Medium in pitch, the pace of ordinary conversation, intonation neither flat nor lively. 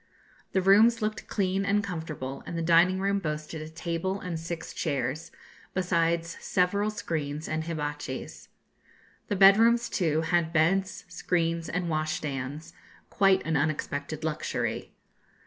No: medium, 165 Hz; slow, 130 wpm; average, 3.5 semitones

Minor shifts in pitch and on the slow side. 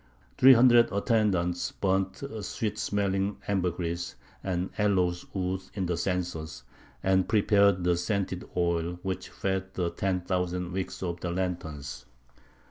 Yes: narrow, 1.9 semitones; slow, 130 wpm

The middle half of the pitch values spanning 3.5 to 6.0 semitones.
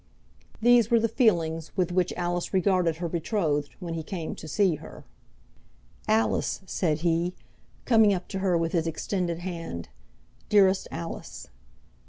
No: average, 3.1 semitones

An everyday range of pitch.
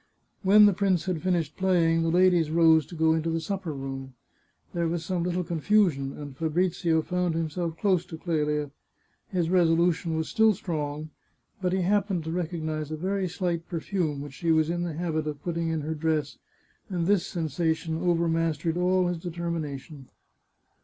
No: narrow, 2.2 semitones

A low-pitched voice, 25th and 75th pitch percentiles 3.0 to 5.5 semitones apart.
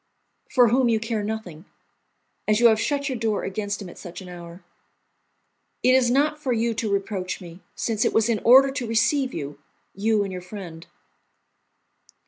No: high, 220 Hz; average, 4.3 semitones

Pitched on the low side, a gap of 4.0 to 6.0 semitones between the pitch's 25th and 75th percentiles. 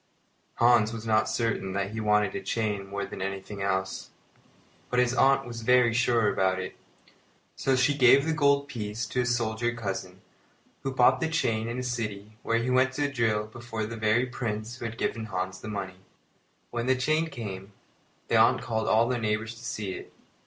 No: low, 115 Hz; average, 2.9 semitones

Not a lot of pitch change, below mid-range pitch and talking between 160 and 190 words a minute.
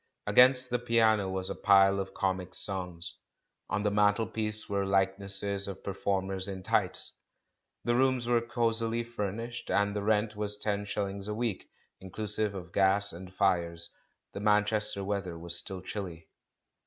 Yes: narrow, 2.2 semitones; low, 100 Hz; average, 165 wpm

